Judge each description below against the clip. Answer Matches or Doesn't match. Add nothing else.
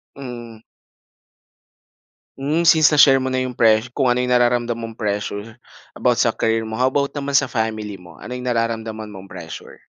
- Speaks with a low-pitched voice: Matches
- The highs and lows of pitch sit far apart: Doesn't match